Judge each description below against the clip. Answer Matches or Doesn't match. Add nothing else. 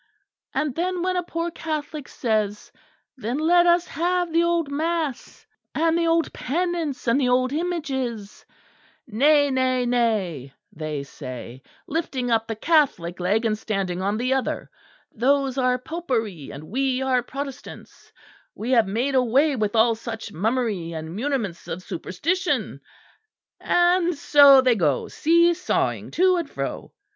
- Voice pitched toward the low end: Doesn't match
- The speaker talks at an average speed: Matches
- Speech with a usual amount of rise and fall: Doesn't match